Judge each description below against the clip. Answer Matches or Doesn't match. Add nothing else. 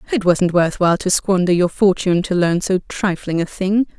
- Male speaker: Doesn't match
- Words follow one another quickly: Matches